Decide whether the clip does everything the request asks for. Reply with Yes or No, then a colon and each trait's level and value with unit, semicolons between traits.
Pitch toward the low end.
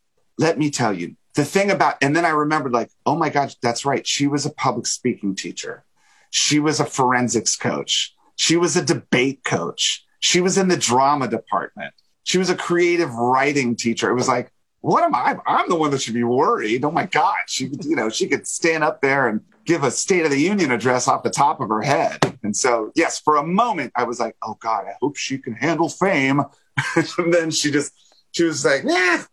No: medium, 150 Hz